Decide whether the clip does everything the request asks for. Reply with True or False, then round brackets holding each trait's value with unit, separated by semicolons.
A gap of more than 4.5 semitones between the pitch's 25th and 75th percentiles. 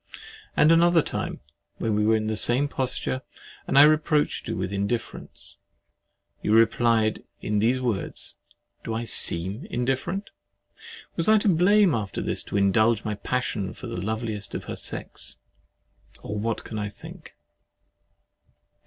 True (5.1 semitones)